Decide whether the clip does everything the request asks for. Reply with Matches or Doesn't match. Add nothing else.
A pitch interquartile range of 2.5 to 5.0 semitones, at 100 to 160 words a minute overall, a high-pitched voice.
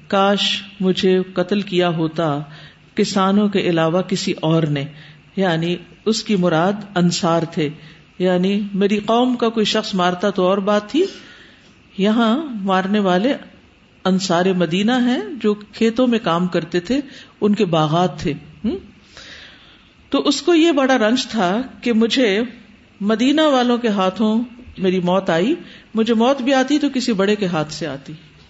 Matches